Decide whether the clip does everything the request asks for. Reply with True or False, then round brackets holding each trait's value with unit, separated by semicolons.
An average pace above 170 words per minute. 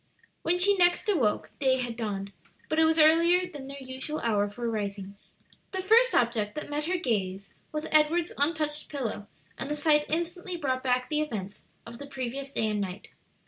True (185 wpm)